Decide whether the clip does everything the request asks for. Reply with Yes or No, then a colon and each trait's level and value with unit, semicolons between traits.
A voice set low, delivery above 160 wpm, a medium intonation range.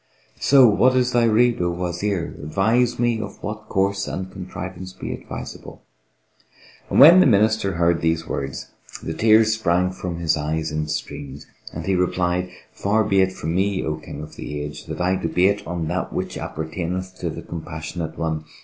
Yes: very low, 90 Hz; average, 175 wpm; average, 4.3 semitones